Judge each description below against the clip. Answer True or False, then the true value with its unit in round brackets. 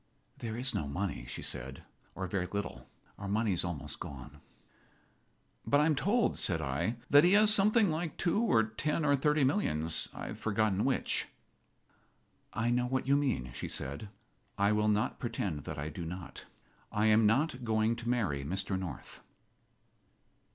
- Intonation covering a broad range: True (7.7 semitones)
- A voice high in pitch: False (110 Hz)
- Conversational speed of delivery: True (170 wpm)